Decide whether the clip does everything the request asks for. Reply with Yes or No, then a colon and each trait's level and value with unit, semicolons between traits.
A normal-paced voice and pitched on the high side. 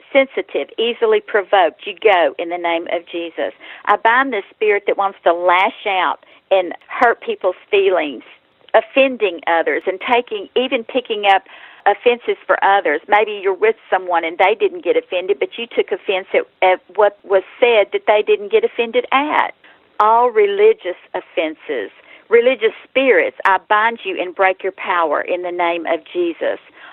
Yes: average, 165 wpm; high, 240 Hz